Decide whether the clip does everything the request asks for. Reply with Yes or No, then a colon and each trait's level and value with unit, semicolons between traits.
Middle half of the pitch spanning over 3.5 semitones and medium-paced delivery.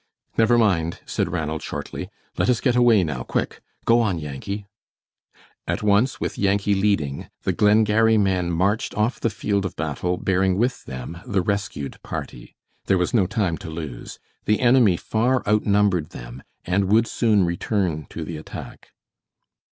Yes: average, 4.4 semitones; average, 160 wpm